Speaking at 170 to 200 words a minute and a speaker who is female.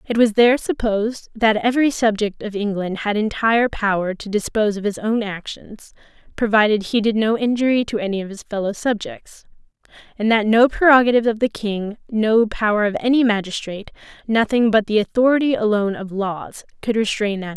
Yes: average, 180 wpm; female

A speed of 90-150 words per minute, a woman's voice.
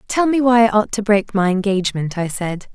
No: fast, 240 wpm; female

